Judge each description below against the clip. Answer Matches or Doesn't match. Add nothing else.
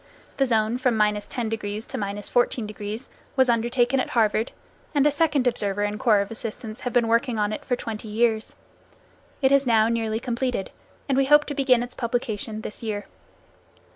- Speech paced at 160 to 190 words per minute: Matches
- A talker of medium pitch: Doesn't match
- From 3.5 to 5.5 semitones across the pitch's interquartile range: Doesn't match